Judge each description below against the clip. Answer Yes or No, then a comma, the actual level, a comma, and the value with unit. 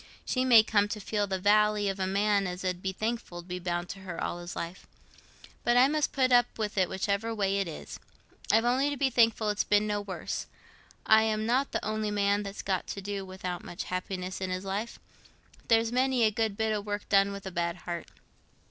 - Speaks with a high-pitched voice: Yes, high, 205 Hz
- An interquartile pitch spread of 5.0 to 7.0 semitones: No, average, 2.8 semitones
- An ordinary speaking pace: No, fast, 220 wpm